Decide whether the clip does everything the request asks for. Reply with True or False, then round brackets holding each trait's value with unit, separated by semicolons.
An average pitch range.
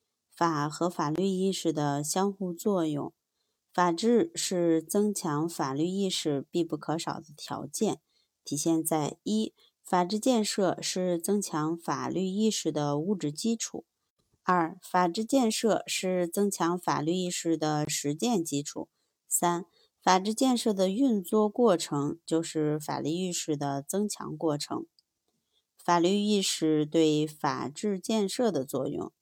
True (4.5 semitones)